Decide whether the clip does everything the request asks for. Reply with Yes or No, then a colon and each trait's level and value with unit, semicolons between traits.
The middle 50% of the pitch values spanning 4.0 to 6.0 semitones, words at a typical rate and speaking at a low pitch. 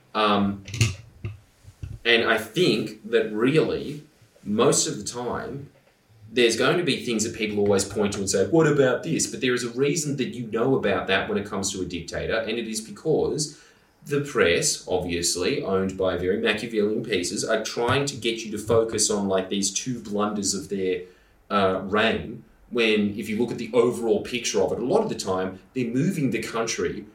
No: average, 3.4 semitones; average, 195 wpm; low, 110 Hz